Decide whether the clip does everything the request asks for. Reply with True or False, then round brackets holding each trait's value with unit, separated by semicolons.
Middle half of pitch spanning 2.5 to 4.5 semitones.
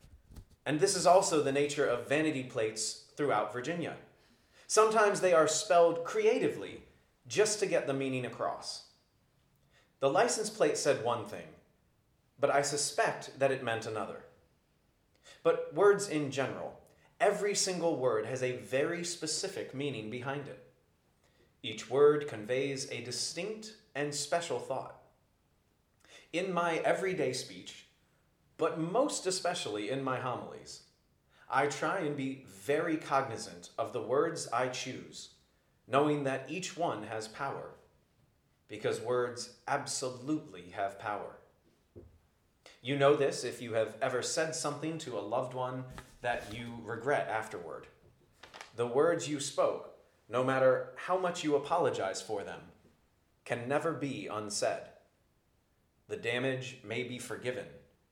False (5.4 semitones)